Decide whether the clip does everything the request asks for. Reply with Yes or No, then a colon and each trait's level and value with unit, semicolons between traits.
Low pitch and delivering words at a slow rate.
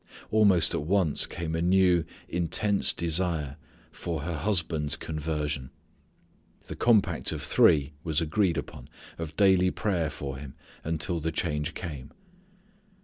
Yes: very low, 80 Hz; slow, 130 wpm